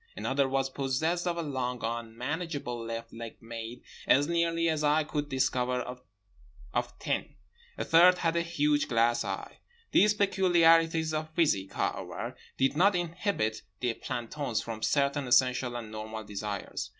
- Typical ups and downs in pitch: No, wide, 5.8 semitones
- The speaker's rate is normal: Yes, average, 145 wpm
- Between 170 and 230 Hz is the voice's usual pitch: No, medium, 140 Hz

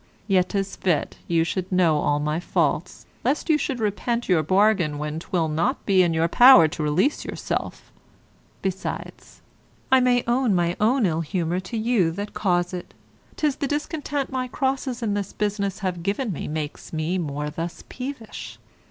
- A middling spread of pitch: No, wide, 6.2 semitones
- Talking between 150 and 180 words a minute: Yes, average, 165 wpm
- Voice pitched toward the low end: No, high, 190 Hz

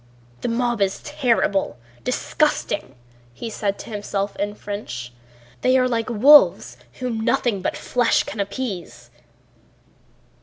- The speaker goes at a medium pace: No, slow, 115 wpm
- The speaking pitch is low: No, high, 210 Hz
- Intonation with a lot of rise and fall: No, average, 3.9 semitones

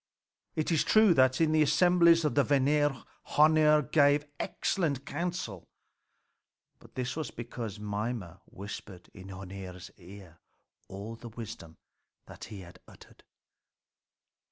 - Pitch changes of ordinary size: No, wide, 7.4 semitones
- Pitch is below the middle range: Yes, low, 125 Hz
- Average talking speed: No, slow, 120 wpm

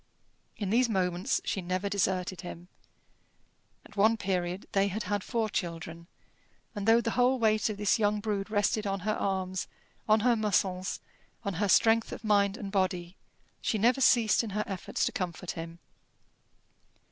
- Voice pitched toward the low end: No, high, 200 Hz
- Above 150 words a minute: Yes, average, 165 wpm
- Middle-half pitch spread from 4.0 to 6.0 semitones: No, average, 2.9 semitones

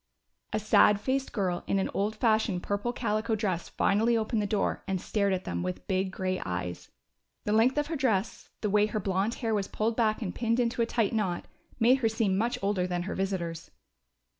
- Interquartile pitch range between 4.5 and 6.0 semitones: No, average, 3.2 semitones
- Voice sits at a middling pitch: No, high, 210 Hz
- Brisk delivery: Yes, fast, 210 wpm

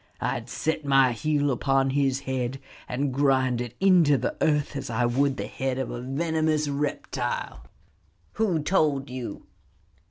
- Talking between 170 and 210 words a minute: No, average, 155 wpm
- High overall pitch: No, low, 135 Hz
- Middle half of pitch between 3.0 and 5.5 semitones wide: No, narrow, 2.5 semitones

